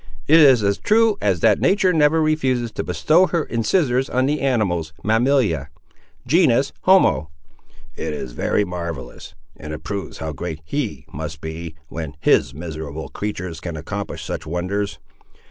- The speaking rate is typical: Yes, average, 150 wpm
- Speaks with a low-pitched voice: Yes, low, 100 Hz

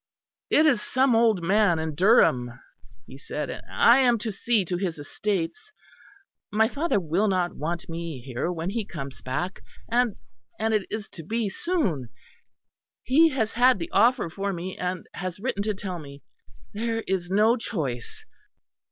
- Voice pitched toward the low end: No, high, 195 Hz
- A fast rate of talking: No, average, 165 wpm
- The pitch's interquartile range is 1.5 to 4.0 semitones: No, wide, 5.4 semitones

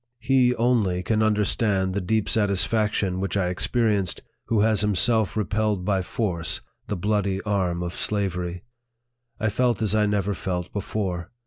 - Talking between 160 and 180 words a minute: No, average, 145 wpm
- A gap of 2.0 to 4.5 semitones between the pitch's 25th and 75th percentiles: Yes, average, 2.8 semitones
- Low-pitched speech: Yes, low, 105 Hz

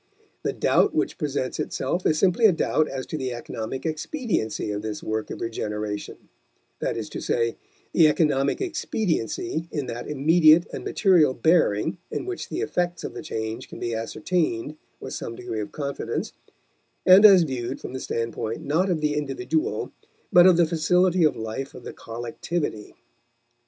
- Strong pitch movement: Yes, wide, 6.8 semitones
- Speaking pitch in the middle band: Yes, medium, 150 Hz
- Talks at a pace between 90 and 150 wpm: No, average, 165 wpm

